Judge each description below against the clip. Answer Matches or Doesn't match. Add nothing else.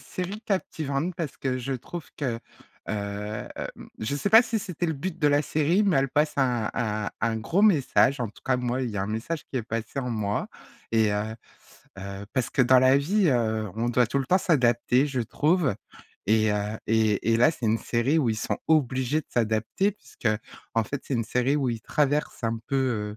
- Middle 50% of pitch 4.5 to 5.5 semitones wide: Matches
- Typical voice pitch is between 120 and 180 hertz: Matches